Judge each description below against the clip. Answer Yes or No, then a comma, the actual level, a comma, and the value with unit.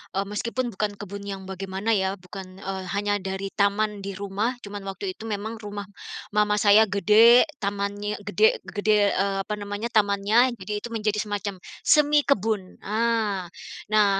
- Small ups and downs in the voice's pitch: Yes, narrow, 1.6 semitones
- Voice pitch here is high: Yes, high, 205 Hz